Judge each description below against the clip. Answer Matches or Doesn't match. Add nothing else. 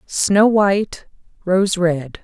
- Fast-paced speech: Doesn't match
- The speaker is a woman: Matches